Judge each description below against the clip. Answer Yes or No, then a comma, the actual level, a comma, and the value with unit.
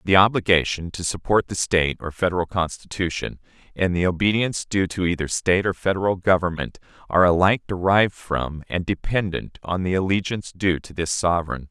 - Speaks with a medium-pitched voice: No, very low, 90 Hz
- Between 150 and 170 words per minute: Yes, average, 165 wpm